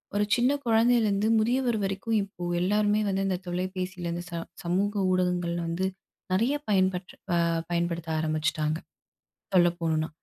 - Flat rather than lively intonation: No, average, 3.4 semitones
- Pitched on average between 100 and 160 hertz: No, medium, 185 Hz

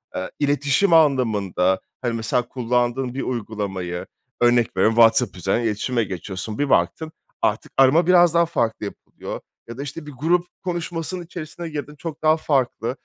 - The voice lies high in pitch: No, low, 130 Hz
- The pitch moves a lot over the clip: Yes, wide, 5.9 semitones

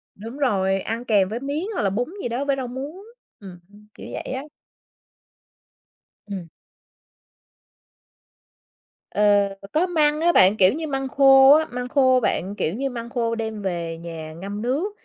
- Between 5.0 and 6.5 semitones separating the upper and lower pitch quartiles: Yes, wide, 5.6 semitones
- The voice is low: No, high, 235 Hz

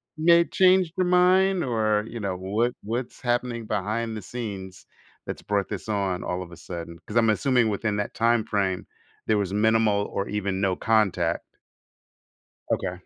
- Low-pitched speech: Yes, low, 110 Hz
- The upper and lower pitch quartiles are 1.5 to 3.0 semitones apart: No, average, 3.5 semitones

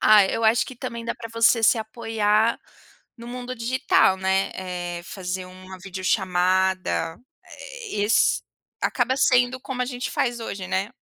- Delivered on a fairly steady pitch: No, average, 4.3 semitones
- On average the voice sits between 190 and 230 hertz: Yes, high, 215 Hz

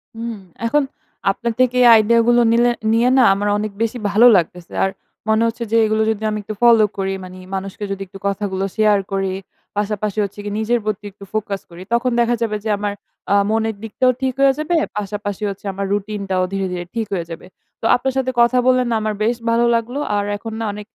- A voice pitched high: Yes, high, 215 Hz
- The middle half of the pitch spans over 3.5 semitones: No, average, 2.9 semitones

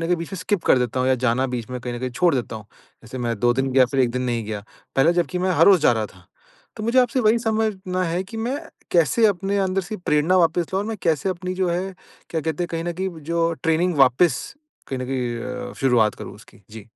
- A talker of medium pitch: Yes, medium, 165 Hz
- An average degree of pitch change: No, wide, 6.8 semitones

